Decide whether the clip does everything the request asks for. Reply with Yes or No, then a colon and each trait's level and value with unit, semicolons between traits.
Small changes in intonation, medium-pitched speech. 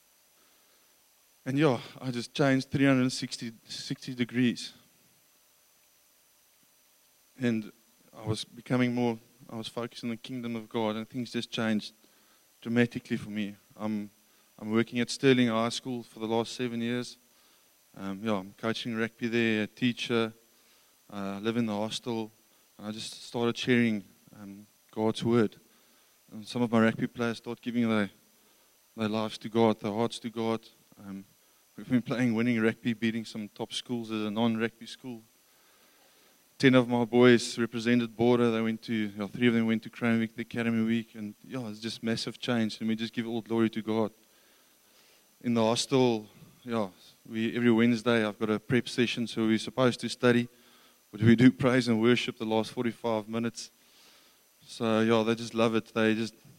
No: narrow, 1.5 semitones; low, 115 Hz